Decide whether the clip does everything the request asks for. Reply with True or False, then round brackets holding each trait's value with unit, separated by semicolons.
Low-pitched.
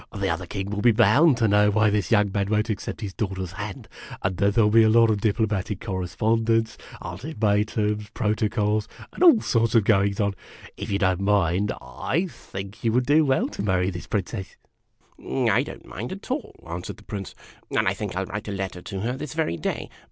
True (105 Hz)